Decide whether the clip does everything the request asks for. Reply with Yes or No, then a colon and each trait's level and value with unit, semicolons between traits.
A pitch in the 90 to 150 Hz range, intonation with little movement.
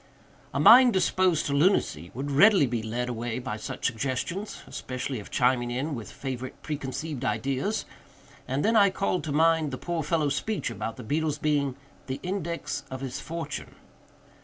No: medium, 140 Hz; average, 4.7 semitones